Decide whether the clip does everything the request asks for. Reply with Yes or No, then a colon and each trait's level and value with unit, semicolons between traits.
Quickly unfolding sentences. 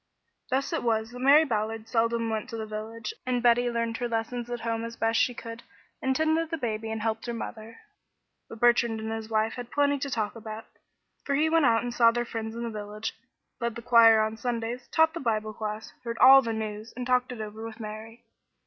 Yes: fast, 225 wpm